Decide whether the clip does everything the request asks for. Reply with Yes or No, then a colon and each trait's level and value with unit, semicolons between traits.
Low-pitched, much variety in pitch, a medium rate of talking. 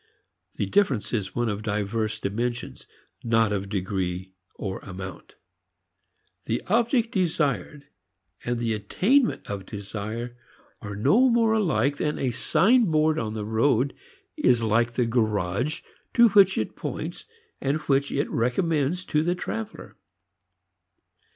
No: low, 120 Hz; wide, 7.5 semitones; slow, 125 wpm